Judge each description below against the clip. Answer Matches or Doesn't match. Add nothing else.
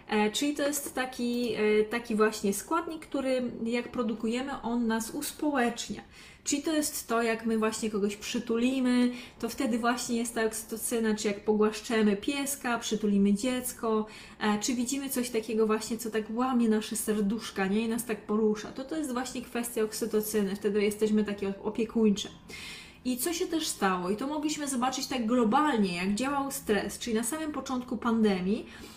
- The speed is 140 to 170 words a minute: Matches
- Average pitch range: Matches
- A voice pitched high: Matches